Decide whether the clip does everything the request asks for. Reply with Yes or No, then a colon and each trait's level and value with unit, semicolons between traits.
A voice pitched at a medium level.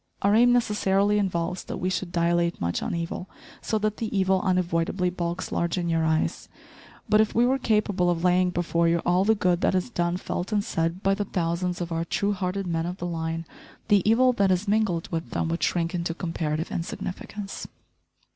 Yes: medium, 180 Hz